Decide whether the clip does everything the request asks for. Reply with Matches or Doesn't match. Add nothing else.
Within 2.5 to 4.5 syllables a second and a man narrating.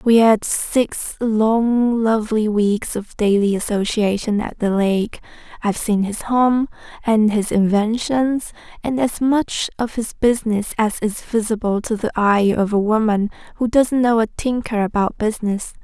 Doesn't match